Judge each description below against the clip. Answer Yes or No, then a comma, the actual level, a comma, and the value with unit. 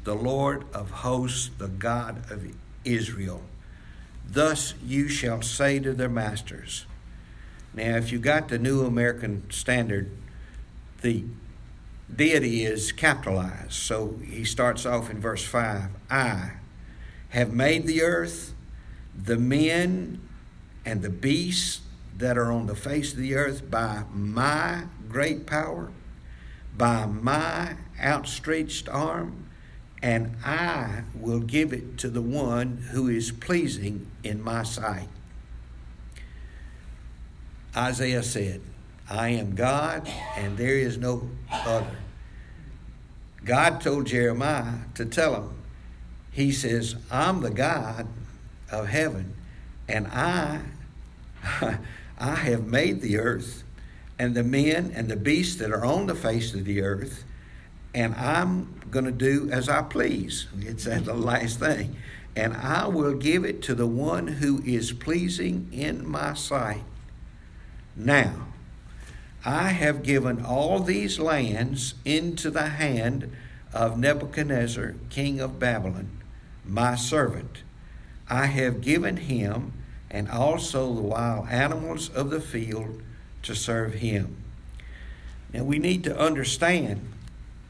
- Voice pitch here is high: No, low, 120 Hz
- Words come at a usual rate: No, slow, 125 wpm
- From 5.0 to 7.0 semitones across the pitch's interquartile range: Yes, average, 5.3 semitones